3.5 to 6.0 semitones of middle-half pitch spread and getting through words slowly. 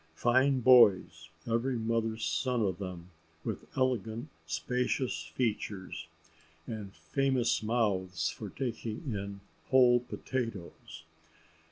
Yes: average, 4.4 semitones; slow, 95 wpm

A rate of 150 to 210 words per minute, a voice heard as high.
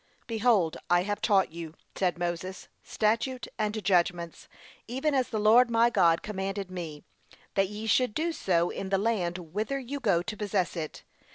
Yes: average, 170 wpm; high, 200 Hz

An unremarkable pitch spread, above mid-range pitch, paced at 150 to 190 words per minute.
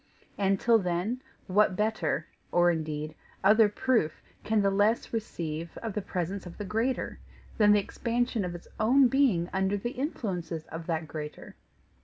Yes: average, 4.6 semitones; high, 195 Hz; average, 160 wpm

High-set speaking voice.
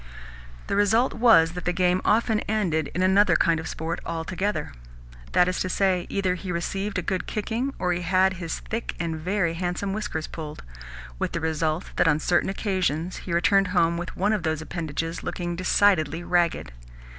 No: medium, 180 Hz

